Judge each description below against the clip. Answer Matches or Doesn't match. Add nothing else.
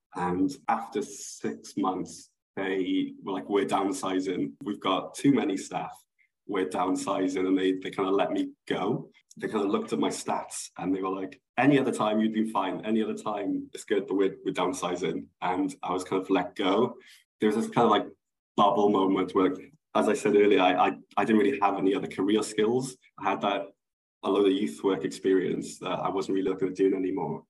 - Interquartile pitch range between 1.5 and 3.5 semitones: Matches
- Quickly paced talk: Matches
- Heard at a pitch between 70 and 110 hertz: Matches